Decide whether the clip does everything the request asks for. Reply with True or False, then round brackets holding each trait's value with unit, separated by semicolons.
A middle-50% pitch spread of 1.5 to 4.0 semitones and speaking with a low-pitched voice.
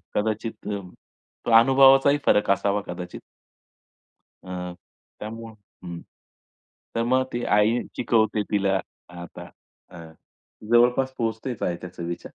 False (4.7 semitones; 110 Hz)